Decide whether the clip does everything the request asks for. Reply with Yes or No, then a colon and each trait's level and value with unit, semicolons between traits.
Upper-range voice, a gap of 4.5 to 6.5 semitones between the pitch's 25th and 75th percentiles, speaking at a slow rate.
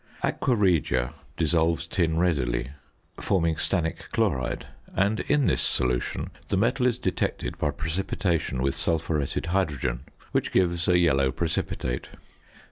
No: very low, 80 Hz; average, 5.3 semitones; slow, 125 wpm